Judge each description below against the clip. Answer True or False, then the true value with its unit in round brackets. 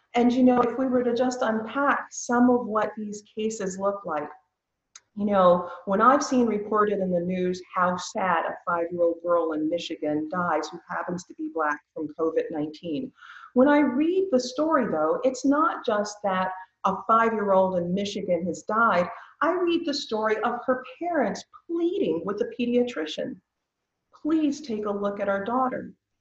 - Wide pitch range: True (6.2 semitones)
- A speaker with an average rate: True (170 wpm)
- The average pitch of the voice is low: False (210 Hz)